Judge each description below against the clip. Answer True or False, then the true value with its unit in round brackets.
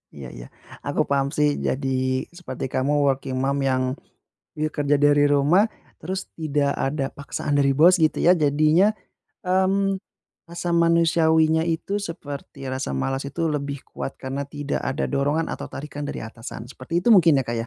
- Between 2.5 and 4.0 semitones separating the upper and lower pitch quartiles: True (3.4 semitones)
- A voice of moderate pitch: True (145 Hz)